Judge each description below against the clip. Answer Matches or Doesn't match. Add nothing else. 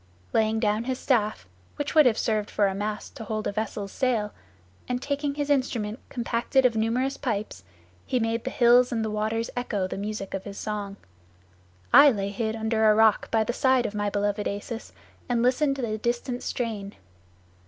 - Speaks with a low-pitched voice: Doesn't match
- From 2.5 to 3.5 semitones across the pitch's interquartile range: Matches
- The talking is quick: Doesn't match